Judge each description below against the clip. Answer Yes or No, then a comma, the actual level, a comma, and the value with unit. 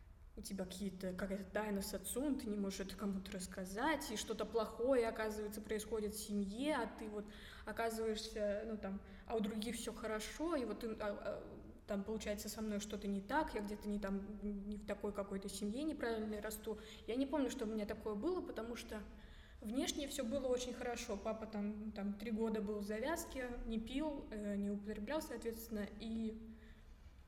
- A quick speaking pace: Yes, fast, 175 wpm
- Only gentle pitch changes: Yes, narrow, 1.9 semitones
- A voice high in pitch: Yes, high, 215 Hz